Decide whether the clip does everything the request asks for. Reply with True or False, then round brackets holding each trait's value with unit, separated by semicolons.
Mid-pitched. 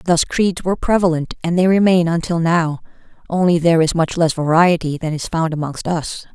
True (170 Hz)